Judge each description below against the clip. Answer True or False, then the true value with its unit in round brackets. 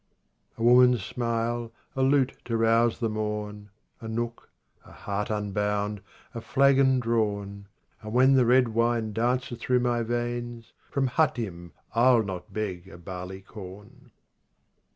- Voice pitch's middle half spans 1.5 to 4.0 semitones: True (2.8 semitones)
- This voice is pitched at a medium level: False (115 Hz)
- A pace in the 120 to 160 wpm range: True (145 wpm)